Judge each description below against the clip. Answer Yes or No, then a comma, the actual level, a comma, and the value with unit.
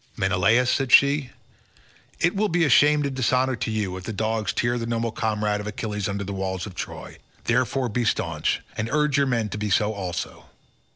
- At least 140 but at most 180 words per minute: No, average, 190 wpm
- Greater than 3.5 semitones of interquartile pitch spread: Yes, average, 4.0 semitones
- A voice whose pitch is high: No, low, 115 Hz